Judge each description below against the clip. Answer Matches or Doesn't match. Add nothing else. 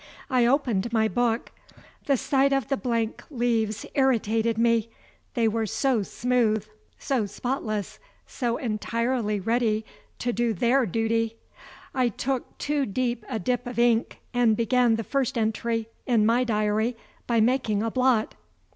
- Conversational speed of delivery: Matches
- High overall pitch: Matches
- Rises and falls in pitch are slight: Matches